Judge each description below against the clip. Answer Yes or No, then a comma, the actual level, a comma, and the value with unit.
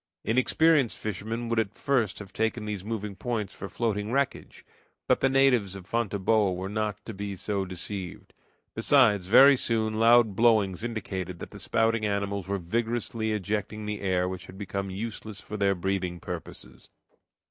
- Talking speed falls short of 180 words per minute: Yes, average, 160 wpm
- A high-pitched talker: No, low, 105 Hz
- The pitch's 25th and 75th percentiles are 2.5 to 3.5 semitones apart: Yes, average, 2.8 semitones